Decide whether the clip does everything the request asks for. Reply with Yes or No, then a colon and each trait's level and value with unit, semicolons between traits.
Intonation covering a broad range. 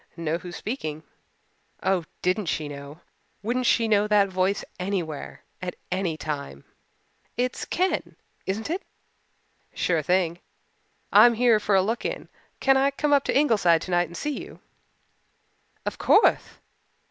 Yes: wide, 5.8 semitones